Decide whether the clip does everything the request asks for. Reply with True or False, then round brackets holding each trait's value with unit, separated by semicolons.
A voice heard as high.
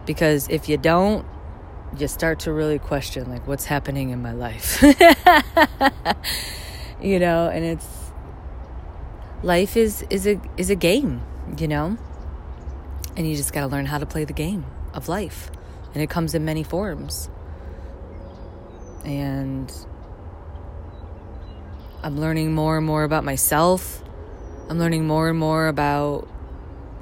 False (140 Hz)